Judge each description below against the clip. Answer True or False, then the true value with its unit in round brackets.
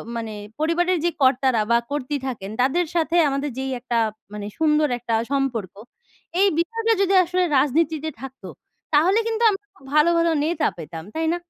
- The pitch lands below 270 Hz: False (300 Hz)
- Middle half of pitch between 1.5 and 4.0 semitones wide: False (5.1 semitones)